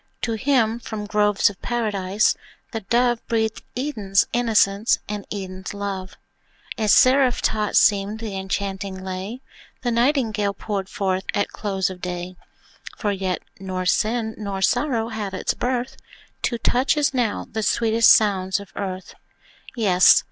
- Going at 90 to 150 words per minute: Yes, average, 140 wpm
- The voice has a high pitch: Yes, high, 210 Hz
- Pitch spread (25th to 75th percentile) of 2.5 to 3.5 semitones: Yes, average, 3.2 semitones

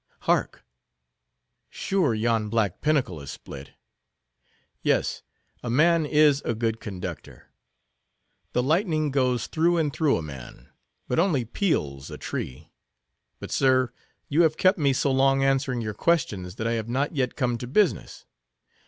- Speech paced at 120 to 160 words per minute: Yes, average, 145 wpm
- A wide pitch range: Yes, wide, 5.7 semitones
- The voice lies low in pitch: Yes, low, 130 Hz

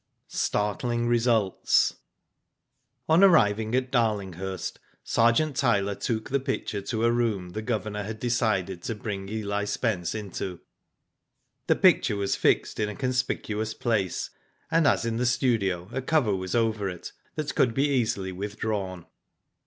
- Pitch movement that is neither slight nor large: Yes, average, 3.3 semitones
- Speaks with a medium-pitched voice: No, low, 110 Hz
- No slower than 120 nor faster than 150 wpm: Yes, average, 140 wpm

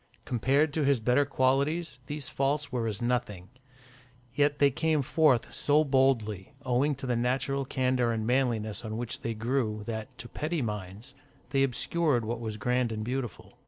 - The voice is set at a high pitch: No, low, 125 Hz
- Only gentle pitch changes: No, average, 3.5 semitones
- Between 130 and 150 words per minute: No, average, 165 wpm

